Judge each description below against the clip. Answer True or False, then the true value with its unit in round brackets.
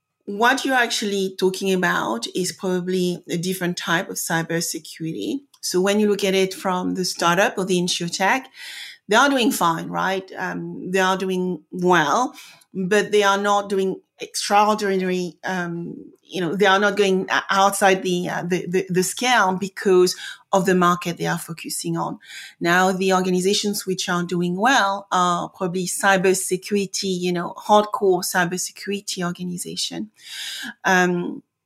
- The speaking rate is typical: True (150 wpm)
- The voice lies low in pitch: False (185 Hz)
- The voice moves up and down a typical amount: False (2.0 semitones)